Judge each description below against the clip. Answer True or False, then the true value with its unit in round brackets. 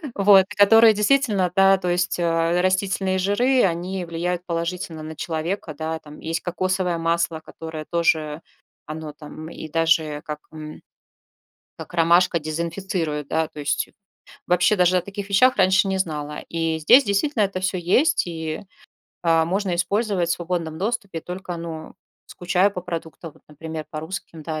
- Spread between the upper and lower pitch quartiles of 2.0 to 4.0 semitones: True (3.0 semitones)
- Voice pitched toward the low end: False (175 Hz)